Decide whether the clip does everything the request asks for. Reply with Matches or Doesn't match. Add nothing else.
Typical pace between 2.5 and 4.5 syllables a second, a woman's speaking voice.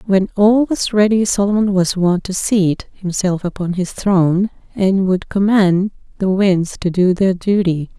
Matches